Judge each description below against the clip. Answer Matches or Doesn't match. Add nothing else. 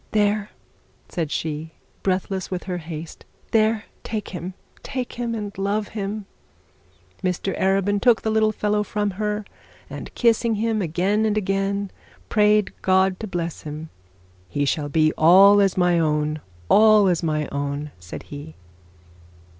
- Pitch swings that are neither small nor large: Matches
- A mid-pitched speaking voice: Doesn't match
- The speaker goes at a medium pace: Matches